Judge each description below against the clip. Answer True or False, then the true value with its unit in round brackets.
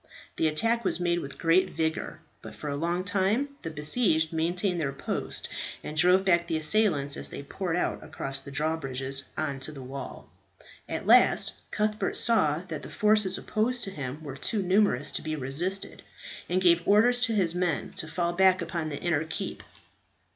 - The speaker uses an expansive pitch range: False (4.2 semitones)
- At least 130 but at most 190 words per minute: True (185 wpm)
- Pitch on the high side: False (170 Hz)